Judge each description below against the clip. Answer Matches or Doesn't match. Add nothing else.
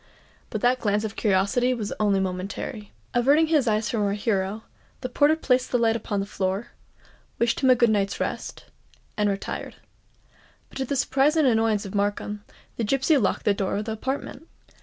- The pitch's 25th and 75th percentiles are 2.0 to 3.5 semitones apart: Doesn't match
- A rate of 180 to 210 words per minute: Matches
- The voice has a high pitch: Matches